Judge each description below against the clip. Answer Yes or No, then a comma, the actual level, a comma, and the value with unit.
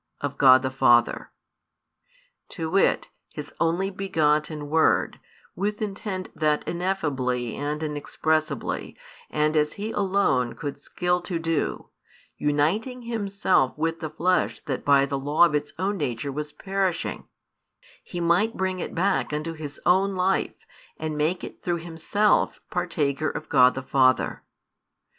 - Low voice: No, medium, 160 Hz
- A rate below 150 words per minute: Yes, average, 140 wpm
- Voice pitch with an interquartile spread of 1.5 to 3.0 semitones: No, average, 4.3 semitones